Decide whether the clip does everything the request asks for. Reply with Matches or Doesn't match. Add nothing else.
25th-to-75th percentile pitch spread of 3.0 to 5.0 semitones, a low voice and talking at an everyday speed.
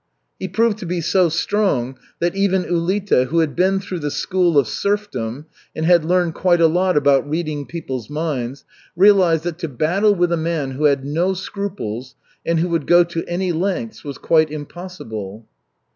Doesn't match